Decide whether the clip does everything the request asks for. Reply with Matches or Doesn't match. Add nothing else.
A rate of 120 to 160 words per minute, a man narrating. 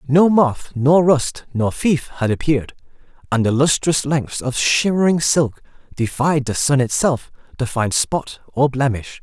Matches